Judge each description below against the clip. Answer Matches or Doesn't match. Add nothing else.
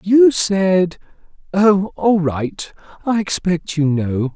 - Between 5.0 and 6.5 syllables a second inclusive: Doesn't match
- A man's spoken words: Matches